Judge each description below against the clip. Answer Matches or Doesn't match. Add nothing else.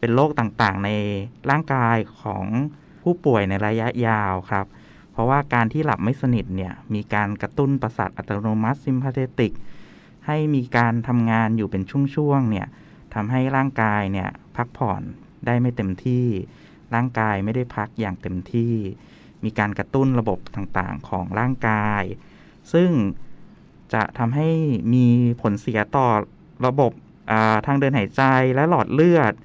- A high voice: Doesn't match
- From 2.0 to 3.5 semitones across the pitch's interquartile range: Doesn't match